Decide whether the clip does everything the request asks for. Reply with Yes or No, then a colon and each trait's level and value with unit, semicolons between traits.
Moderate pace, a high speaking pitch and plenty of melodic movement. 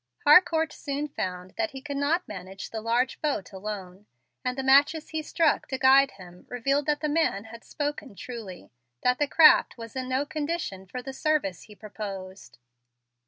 Yes: average, 180 wpm; very high, 260 Hz; wide, 6.2 semitones